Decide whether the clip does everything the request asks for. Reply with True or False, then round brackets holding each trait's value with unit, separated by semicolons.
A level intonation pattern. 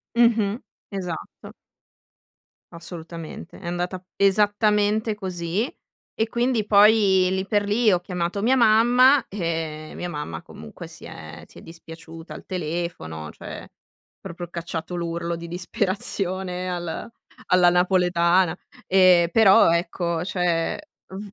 False (3.3 semitones)